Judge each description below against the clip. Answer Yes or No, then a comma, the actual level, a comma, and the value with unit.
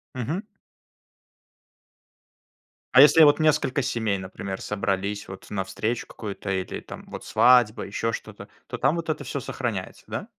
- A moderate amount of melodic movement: No, wide, 6.0 semitones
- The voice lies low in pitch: Yes, low, 115 Hz